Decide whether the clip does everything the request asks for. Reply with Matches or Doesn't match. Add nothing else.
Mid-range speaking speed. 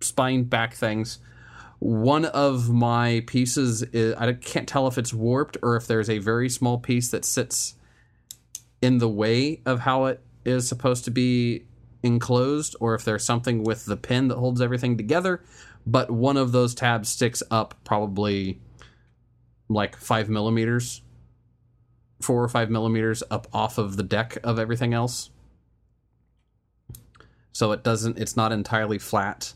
Matches